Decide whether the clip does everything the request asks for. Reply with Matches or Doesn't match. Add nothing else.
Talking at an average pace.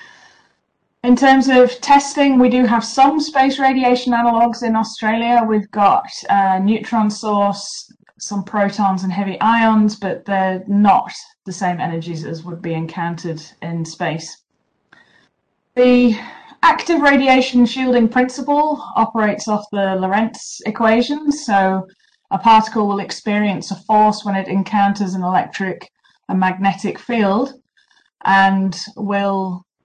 Doesn't match